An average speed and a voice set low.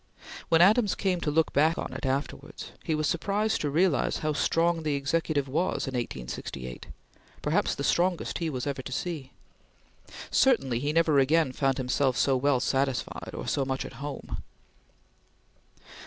No: average, 160 wpm; medium, 145 Hz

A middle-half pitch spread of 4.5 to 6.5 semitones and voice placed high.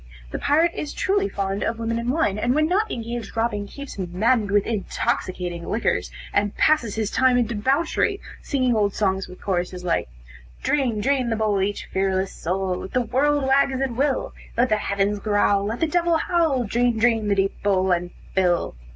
Yes: average, 5.2 semitones; high, 225 Hz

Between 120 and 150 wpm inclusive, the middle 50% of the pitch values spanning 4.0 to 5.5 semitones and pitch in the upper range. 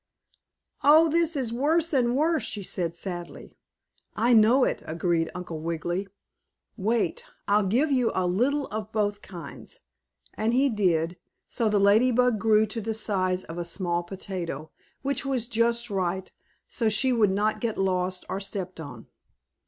No: average, 160 wpm; average, 4.9 semitones; high, 210 Hz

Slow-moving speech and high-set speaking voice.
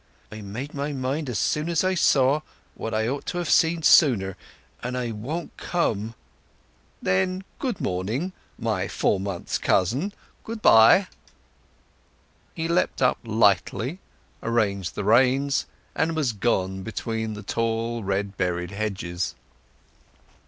No: slow, 130 wpm; low, 115 Hz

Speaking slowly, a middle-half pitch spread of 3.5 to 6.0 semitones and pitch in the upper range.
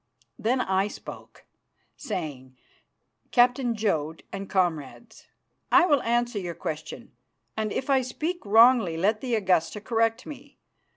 Yes: slow, 125 wpm; wide, 5.4 semitones; high, 220 Hz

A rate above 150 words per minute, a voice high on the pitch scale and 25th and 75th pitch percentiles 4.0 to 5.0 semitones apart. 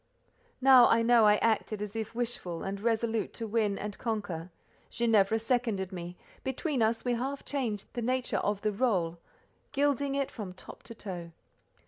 No: average, 165 wpm; high, 225 Hz; average, 3.4 semitones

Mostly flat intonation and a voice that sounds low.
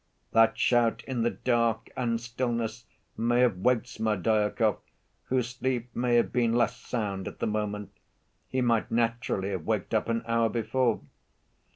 Yes: narrow, 1.5 semitones; low, 115 Hz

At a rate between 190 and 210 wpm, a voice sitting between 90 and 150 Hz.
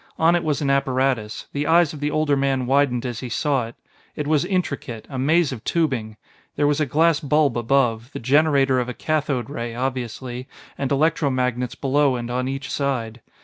Yes: average, 195 wpm; low, 135 Hz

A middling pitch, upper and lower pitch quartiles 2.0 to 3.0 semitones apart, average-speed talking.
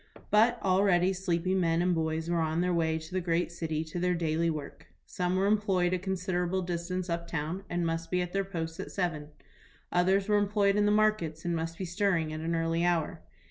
No: medium, 175 Hz; narrow, 2.4 semitones; fast, 215 wpm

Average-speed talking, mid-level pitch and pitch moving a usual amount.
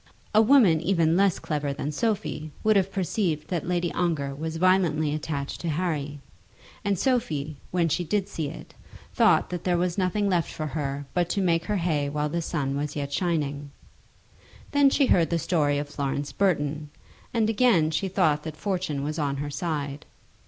Yes: average, 180 wpm; medium, 160 Hz; average, 3.9 semitones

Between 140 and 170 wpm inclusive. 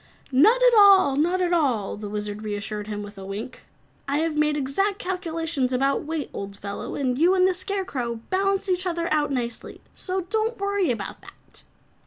No: average, 180 wpm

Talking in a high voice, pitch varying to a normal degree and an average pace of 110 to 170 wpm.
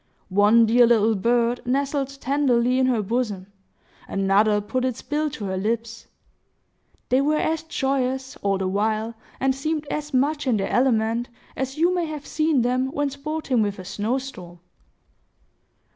Yes: very high, 250 Hz; average, 4.3 semitones; average, 160 wpm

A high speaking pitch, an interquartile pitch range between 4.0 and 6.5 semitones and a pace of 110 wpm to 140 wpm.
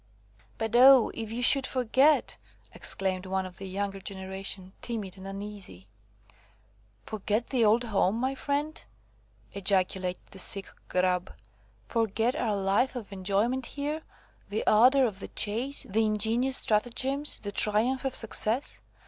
Yes: high, 215 Hz; average, 4.4 semitones; slow, 135 wpm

